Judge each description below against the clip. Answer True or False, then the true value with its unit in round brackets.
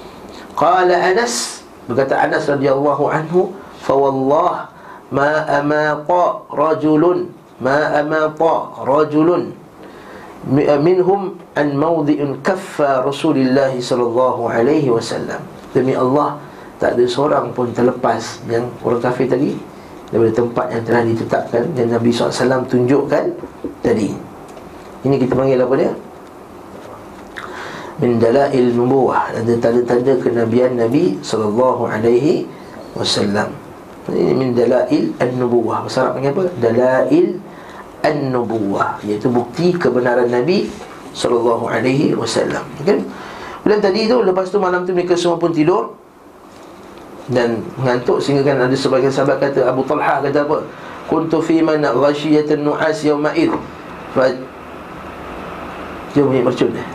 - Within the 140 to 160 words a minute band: False (115 wpm)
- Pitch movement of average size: True (4.3 semitones)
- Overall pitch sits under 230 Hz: True (135 Hz)